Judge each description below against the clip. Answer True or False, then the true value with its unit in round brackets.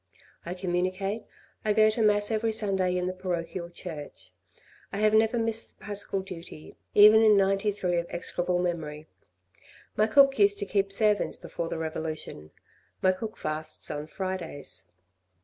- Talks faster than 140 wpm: True (150 wpm)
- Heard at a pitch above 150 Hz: True (190 Hz)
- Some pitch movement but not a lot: True (3.6 semitones)